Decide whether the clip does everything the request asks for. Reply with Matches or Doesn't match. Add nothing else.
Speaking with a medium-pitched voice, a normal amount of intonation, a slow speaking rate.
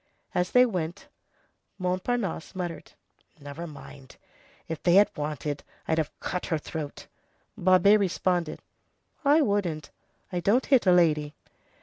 Matches